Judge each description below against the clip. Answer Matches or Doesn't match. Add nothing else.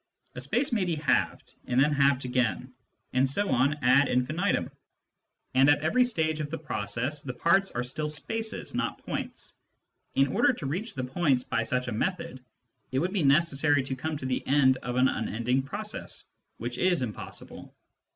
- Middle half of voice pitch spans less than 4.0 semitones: Doesn't match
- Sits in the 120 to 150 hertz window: Matches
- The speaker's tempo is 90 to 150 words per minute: Doesn't match